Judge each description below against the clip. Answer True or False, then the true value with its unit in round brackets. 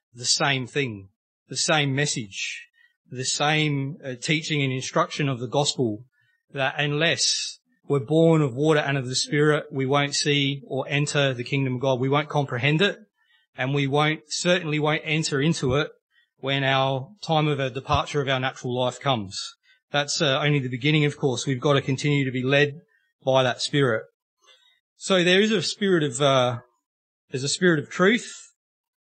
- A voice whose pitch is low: False (145 Hz)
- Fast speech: False (175 wpm)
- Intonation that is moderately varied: True (3.2 semitones)